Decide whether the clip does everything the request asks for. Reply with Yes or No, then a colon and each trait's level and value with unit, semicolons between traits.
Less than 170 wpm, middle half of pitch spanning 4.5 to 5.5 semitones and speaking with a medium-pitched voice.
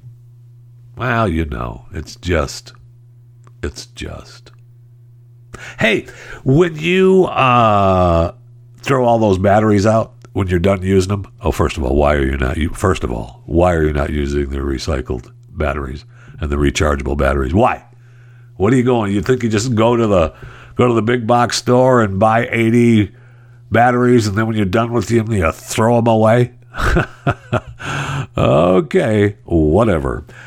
No: average, 160 wpm; average, 4.9 semitones; low, 115 Hz